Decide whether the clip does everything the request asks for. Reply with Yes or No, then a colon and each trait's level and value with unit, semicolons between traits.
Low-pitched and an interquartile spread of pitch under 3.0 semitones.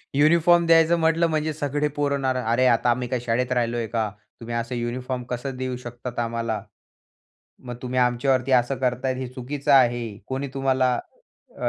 Yes: low, 125 Hz; narrow, 2.5 semitones